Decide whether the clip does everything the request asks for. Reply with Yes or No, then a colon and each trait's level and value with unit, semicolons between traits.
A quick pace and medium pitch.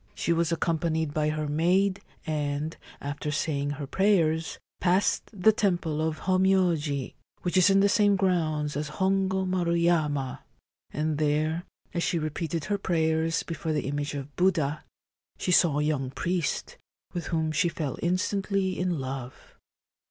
No: average, 150 wpm; medium, 160 Hz